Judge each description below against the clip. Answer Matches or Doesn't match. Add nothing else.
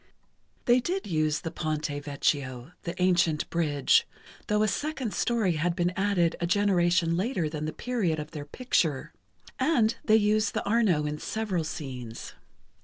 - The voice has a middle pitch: Matches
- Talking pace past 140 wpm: Matches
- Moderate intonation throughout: Doesn't match